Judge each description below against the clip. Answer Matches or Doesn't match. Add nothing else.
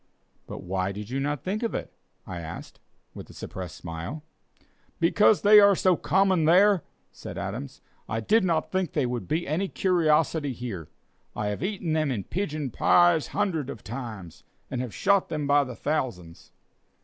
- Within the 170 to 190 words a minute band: Matches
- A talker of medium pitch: Matches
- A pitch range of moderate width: Doesn't match